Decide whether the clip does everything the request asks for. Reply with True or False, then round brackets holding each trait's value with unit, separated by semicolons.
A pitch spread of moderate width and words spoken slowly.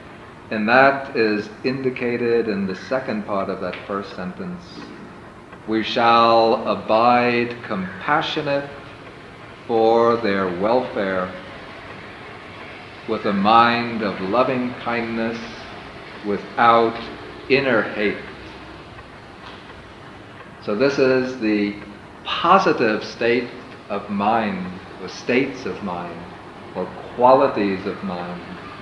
True (3.4 semitones; 90 wpm)